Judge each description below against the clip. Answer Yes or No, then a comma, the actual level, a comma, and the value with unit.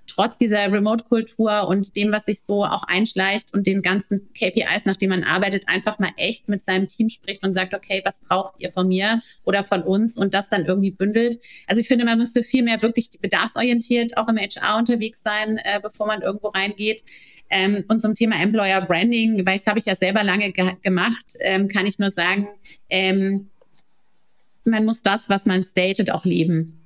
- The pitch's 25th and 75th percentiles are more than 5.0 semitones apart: No, narrow, 2.4 semitones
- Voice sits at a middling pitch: No, high, 200 Hz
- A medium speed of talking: No, fast, 195 wpm